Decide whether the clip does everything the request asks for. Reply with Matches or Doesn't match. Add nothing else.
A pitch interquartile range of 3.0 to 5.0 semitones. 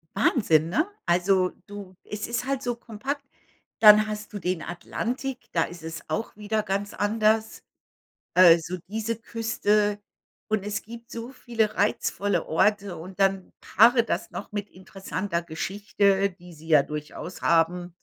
Matches